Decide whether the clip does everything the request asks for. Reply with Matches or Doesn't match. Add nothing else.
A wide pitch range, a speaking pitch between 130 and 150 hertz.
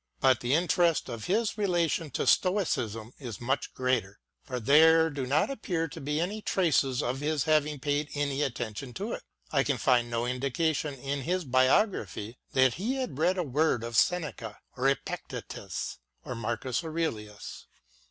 Doesn't match